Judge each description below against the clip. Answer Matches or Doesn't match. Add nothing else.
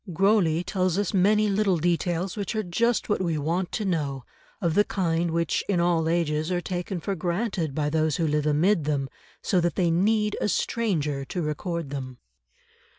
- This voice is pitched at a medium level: Matches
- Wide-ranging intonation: Doesn't match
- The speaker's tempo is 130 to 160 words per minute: Doesn't match